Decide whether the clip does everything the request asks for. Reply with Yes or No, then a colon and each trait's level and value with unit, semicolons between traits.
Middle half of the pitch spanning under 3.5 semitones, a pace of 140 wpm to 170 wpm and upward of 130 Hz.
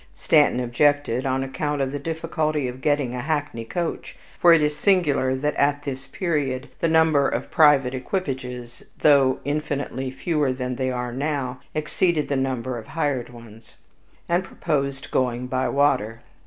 Yes: average, 2.9 semitones; average, 155 wpm; medium, 140 Hz